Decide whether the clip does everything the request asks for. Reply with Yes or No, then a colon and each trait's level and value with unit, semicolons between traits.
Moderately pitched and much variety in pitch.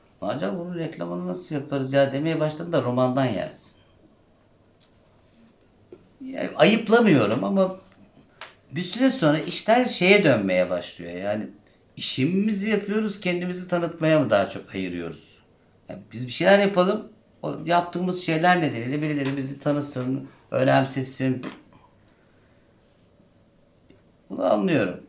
Yes: medium, 155 Hz; wide, 6.0 semitones